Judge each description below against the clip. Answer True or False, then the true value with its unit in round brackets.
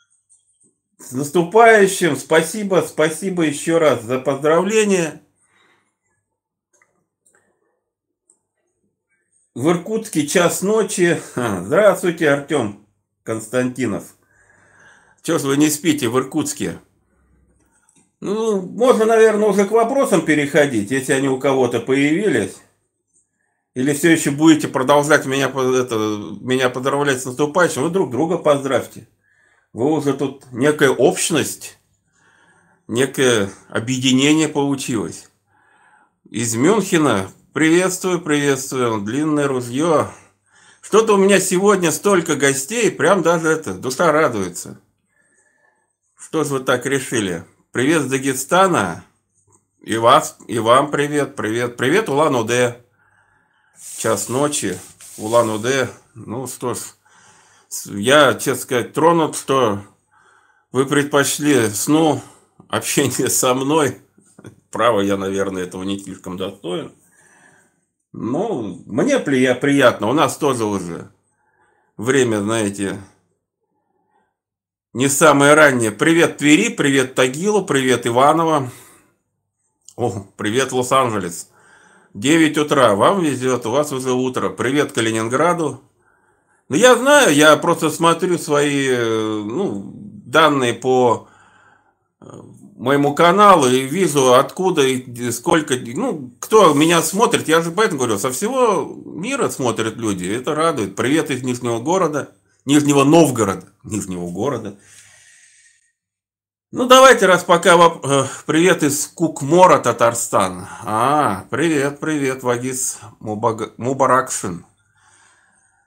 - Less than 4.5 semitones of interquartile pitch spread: False (5.5 semitones)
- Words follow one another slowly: True (100 wpm)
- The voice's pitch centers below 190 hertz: True (140 Hz)